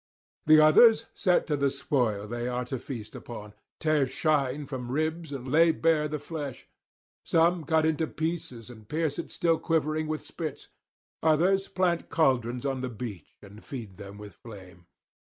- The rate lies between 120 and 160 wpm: No, average, 170 wpm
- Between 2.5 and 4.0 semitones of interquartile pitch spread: No, average, 4.8 semitones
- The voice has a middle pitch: Yes, medium, 145 Hz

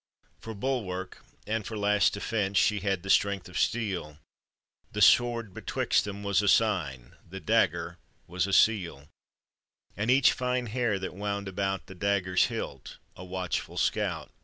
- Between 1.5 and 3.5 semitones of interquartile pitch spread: Yes, average, 2.9 semitones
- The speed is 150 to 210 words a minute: Yes, average, 155 wpm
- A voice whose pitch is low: Yes, low, 100 Hz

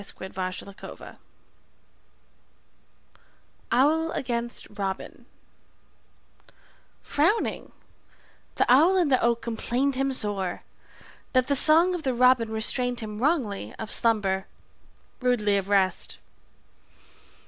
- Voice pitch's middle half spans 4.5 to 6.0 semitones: Yes, average, 4.8 semitones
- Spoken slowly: Yes, slow, 95 wpm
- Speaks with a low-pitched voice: No, high, 240 Hz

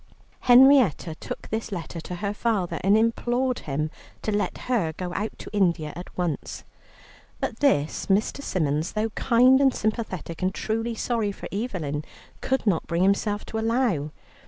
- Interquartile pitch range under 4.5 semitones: No, average, 5.3 semitones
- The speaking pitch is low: No, high, 205 Hz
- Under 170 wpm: Yes, average, 160 wpm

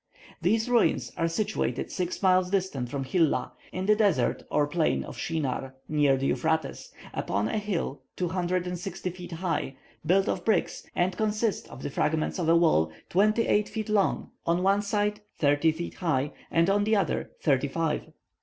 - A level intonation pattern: No, average, 4.5 semitones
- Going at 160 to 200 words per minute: Yes, average, 170 wpm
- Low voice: No, medium, 175 Hz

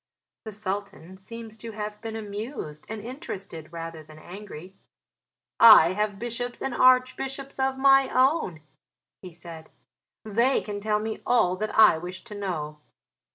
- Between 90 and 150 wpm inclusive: Yes, average, 145 wpm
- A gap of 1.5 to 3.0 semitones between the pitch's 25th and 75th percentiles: No, average, 4.8 semitones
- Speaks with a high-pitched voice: Yes, high, 210 Hz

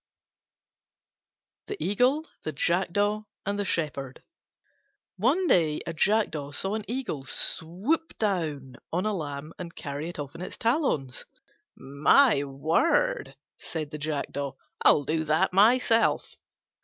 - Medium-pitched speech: Yes, medium, 170 Hz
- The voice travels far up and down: Yes, wide, 6.6 semitones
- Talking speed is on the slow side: Yes, slow, 125 wpm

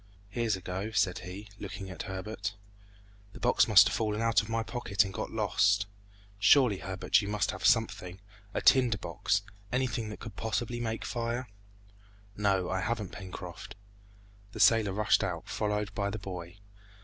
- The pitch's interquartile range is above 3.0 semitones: No, average, 2.7 semitones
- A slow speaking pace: No, average, 165 wpm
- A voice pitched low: Yes, low, 105 Hz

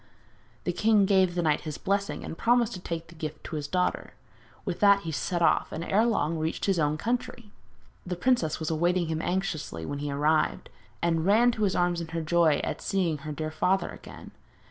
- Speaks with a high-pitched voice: No, medium, 170 Hz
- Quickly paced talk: Yes, fast, 210 wpm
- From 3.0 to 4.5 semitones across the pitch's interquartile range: Yes, average, 3.9 semitones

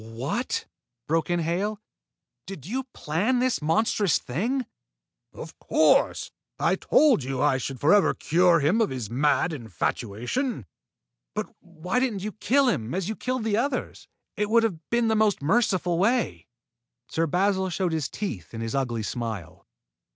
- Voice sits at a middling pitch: Yes, medium, 180 Hz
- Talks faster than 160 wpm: No, average, 155 wpm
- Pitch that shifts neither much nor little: No, wide, 8.4 semitones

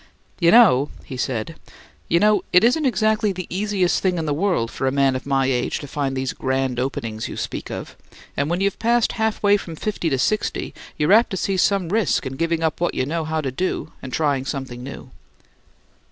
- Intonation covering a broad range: Yes, wide, 6.8 semitones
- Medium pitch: Yes, medium, 160 Hz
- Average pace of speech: No, fast, 215 wpm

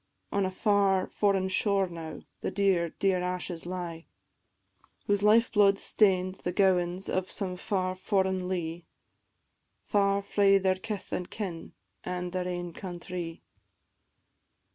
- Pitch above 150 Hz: Yes, medium, 185 Hz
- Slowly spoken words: Yes, slow, 130 wpm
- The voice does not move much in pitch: Yes, narrow, 1.9 semitones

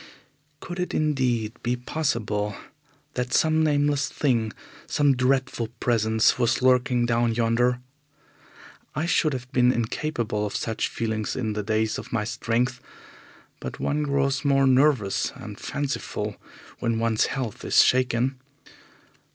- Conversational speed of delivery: No, slow, 130 wpm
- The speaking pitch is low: Yes, low, 125 Hz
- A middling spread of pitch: Yes, average, 3.2 semitones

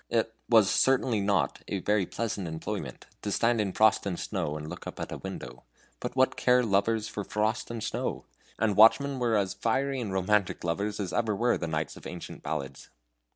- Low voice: Yes, low, 105 Hz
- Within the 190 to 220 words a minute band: Yes, average, 200 wpm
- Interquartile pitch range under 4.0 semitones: Yes, average, 3.6 semitones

